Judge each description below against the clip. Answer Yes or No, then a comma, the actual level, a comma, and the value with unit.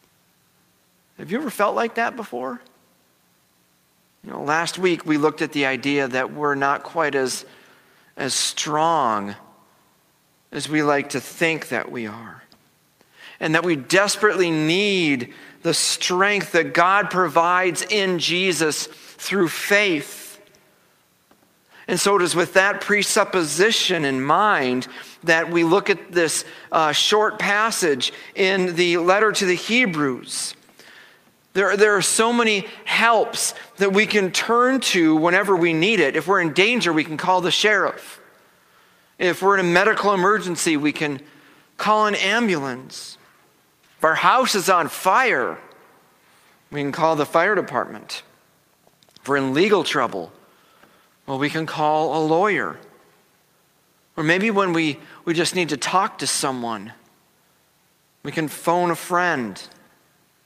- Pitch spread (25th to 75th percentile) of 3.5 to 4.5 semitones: No, average, 4.9 semitones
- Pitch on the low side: No, medium, 170 Hz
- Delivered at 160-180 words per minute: No, average, 140 wpm